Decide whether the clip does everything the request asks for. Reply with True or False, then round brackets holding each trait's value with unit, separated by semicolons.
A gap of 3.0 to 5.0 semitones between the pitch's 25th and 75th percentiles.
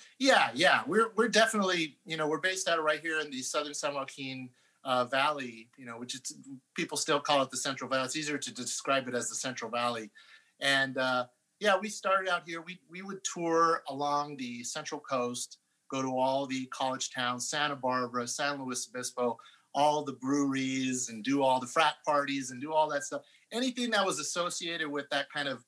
True (3.9 semitones)